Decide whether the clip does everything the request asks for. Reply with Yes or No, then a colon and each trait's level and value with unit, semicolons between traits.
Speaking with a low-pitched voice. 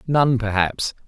Yes: low, 120 Hz